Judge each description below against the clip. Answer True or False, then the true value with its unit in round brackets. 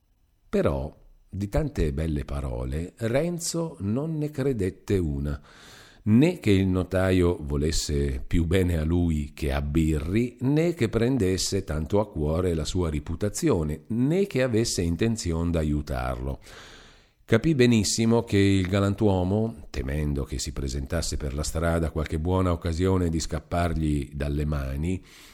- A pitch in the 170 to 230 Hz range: False (85 Hz)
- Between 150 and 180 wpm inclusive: False (130 wpm)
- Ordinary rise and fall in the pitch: False (5.8 semitones)